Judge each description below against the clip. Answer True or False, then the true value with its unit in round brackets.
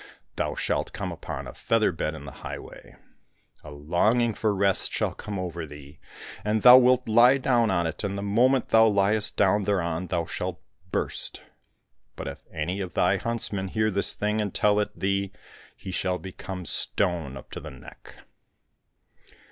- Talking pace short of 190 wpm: True (170 wpm)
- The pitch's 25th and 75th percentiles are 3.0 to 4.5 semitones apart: True (3.7 semitones)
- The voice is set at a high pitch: False (100 Hz)